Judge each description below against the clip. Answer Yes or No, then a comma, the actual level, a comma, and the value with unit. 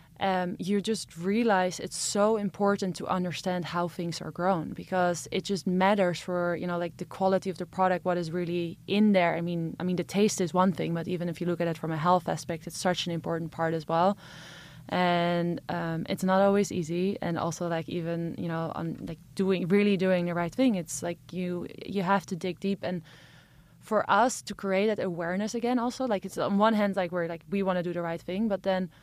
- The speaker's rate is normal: No, fast, 230 wpm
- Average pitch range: No, narrow, 2.3 semitones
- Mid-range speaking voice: Yes, medium, 180 Hz